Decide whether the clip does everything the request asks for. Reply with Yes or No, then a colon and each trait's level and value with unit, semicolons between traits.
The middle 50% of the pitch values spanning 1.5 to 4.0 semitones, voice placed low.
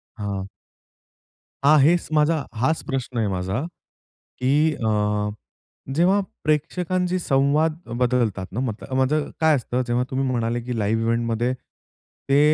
No: average, 4.9 semitones; low, 130 Hz